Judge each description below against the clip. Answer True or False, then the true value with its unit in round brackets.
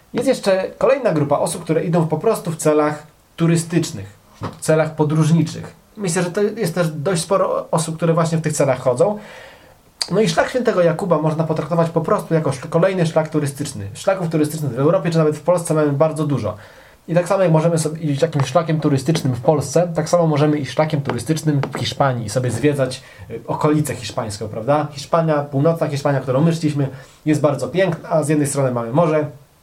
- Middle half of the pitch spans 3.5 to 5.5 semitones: False (2.8 semitones)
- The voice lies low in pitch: False (155 Hz)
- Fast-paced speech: True (190 wpm)